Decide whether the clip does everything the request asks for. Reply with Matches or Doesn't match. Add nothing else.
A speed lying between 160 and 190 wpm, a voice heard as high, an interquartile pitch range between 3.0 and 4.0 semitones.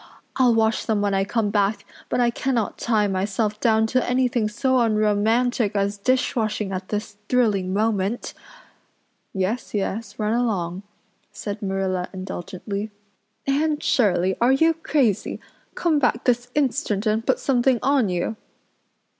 Doesn't match